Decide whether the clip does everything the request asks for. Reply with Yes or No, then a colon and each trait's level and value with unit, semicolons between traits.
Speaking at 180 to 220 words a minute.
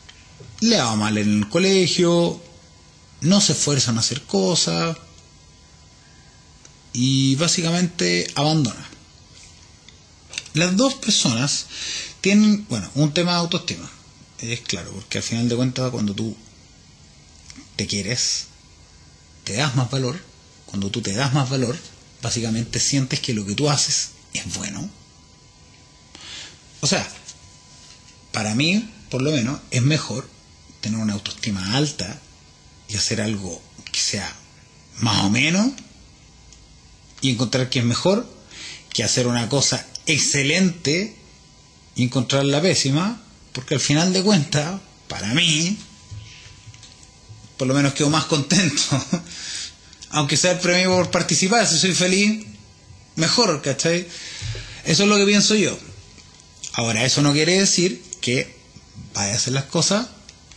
No: average, 130 wpm